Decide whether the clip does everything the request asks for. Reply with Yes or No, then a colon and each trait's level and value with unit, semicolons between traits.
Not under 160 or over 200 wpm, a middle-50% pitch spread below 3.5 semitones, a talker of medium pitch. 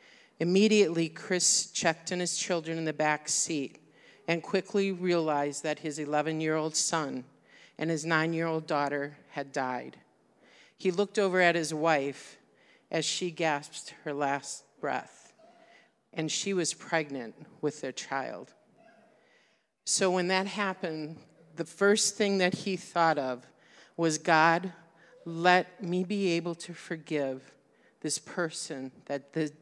No: average, 140 wpm; average, 2.9 semitones; medium, 165 Hz